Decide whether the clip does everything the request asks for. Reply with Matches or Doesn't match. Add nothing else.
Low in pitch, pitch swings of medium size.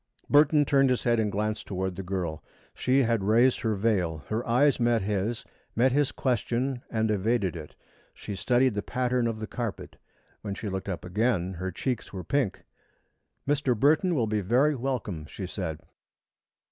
Matches